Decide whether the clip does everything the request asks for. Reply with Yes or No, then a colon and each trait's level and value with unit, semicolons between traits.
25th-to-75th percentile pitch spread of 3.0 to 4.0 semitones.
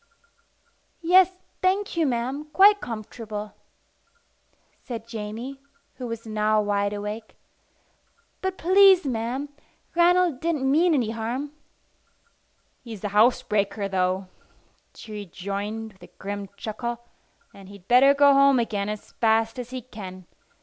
No: average, 4.9 semitones